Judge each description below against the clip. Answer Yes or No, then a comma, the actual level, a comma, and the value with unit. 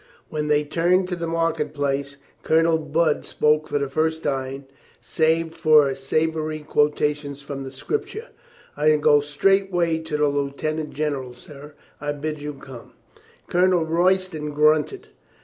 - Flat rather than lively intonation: Yes, narrow, 2.1 semitones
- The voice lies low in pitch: No, medium, 150 Hz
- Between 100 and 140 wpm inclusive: No, average, 150 wpm